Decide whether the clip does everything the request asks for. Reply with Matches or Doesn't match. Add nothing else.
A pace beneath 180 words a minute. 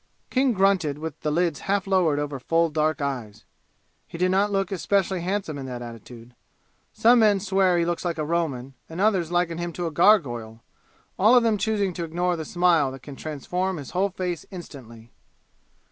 Doesn't match